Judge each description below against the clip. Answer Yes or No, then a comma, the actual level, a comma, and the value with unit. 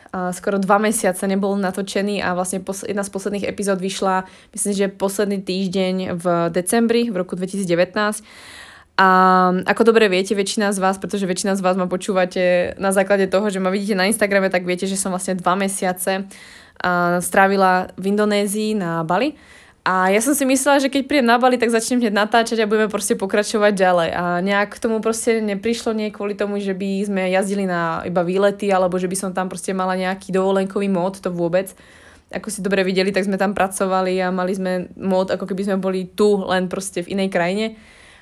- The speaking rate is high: Yes, fast, 195 wpm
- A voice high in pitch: Yes, high, 195 Hz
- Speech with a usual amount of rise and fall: No, narrow, 1.9 semitones